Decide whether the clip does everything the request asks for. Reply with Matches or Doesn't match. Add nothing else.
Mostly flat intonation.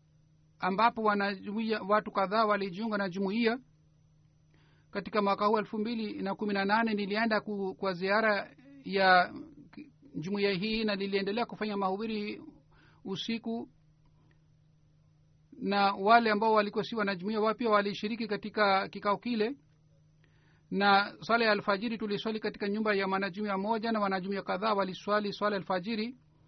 Matches